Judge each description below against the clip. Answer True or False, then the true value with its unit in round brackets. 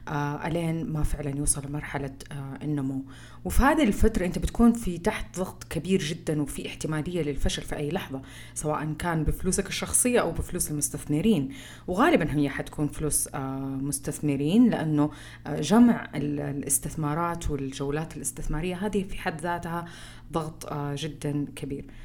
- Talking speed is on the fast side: True (140 wpm)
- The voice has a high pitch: False (150 Hz)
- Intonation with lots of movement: False (3.3 semitones)